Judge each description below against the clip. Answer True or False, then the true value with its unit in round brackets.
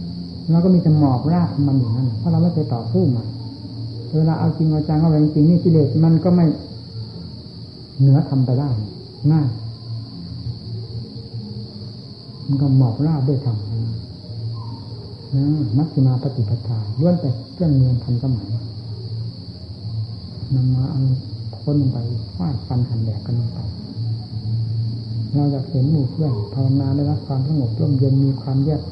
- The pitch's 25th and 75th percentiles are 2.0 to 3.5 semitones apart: False (3.9 semitones)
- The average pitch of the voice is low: True (125 Hz)